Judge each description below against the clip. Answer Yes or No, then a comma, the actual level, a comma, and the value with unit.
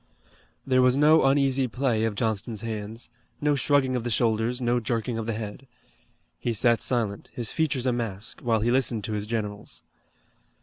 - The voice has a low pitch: Yes, low, 120 Hz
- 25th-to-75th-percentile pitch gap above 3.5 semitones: No, average, 2.7 semitones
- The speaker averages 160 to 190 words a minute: Yes, average, 175 wpm